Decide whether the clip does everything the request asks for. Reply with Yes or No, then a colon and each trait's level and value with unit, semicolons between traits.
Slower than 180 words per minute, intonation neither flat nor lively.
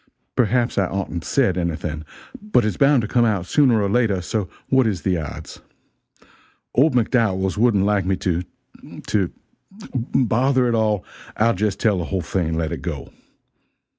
Yes: average, 165 wpm; average, 4.6 semitones